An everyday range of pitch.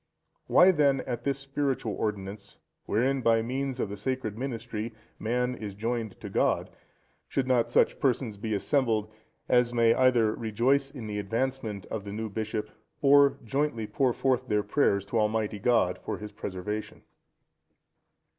Yes: average, 3.6 semitones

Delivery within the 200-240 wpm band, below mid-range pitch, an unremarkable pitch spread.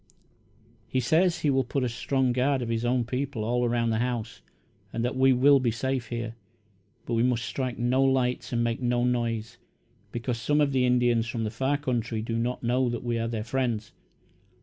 No: fast, 205 wpm; low, 120 Hz; narrow, 2.0 semitones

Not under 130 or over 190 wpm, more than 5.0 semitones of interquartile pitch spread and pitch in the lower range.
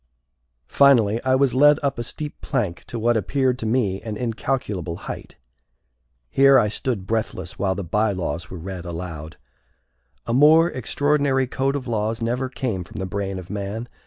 Yes: average, 165 wpm; wide, 5.5 semitones; low, 115 Hz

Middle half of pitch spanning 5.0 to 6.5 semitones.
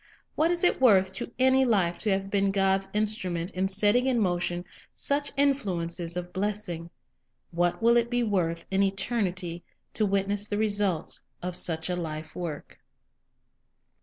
No: average, 3.5 semitones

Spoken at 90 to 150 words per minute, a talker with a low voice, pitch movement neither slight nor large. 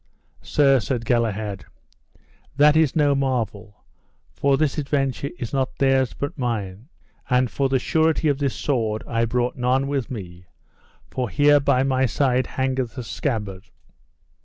Yes: average, 145 wpm; low, 130 Hz; average, 3.4 semitones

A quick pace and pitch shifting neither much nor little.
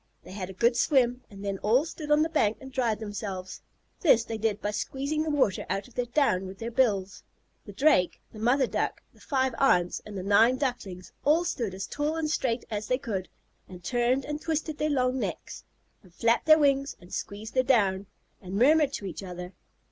No: fast, 210 wpm; wide, 5.8 semitones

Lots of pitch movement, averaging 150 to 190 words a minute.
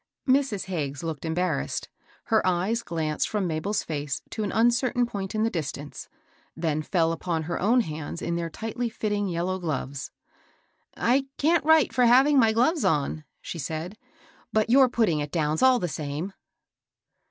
Yes: wide, 6.6 semitones; average, 170 wpm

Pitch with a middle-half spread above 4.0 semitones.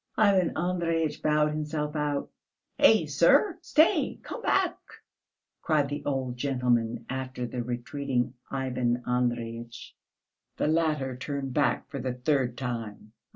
No: average, 3.6 semitones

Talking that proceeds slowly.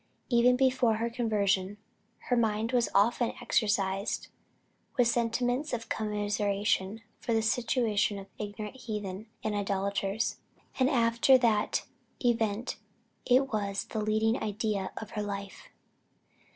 Yes: slow, 120 wpm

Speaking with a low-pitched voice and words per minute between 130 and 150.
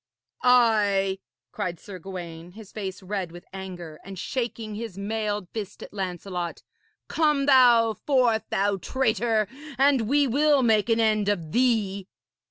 No: high, 210 Hz; average, 140 wpm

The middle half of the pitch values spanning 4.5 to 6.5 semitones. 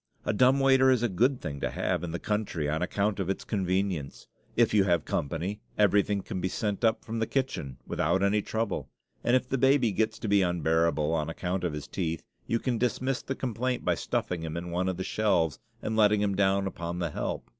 Yes: average, 4.8 semitones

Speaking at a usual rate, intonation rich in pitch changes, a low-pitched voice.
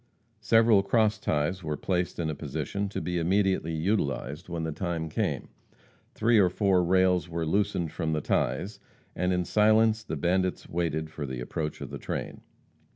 No: average, 170 wpm; average, 3.8 semitones; very low, 90 Hz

